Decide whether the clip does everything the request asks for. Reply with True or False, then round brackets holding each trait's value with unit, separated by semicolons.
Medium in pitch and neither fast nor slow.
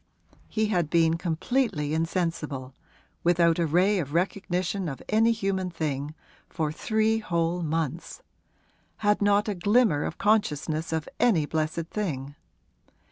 False (170 Hz; 130 wpm)